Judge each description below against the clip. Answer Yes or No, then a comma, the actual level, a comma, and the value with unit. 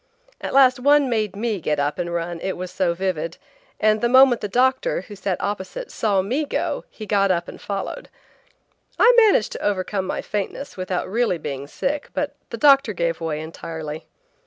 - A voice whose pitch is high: Yes, high, 200 Hz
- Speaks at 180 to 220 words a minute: Yes, average, 185 wpm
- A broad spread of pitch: Yes, wide, 6.3 semitones